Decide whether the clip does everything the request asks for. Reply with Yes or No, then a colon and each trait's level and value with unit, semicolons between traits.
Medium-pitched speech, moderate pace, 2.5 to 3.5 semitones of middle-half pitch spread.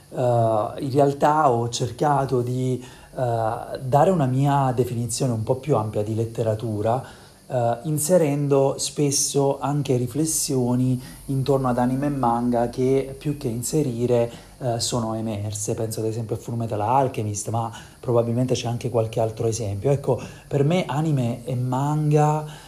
No: low, 125 Hz; average, 140 wpm; average, 3.2 semitones